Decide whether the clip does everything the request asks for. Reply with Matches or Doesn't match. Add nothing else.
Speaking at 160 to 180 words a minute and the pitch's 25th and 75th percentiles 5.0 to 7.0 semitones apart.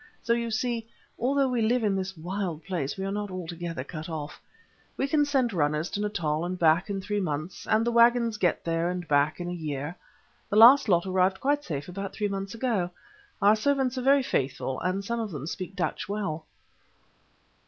Doesn't match